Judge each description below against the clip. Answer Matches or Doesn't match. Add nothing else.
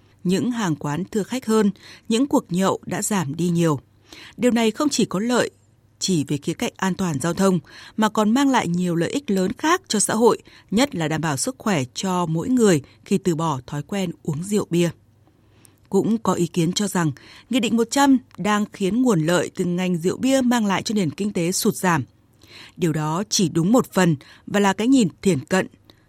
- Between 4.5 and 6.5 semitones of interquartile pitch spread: Matches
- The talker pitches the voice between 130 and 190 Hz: Matches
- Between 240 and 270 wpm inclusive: Doesn't match